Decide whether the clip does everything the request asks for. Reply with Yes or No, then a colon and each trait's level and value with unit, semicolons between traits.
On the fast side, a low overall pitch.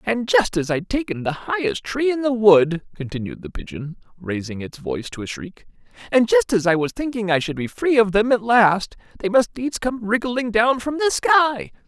No: fast, 215 wpm; high, 190 Hz